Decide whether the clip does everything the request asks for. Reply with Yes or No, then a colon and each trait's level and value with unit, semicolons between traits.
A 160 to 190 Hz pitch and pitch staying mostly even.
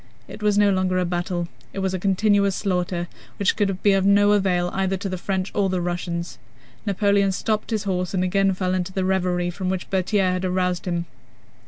Yes: medium, 185 Hz; narrow, 1.6 semitones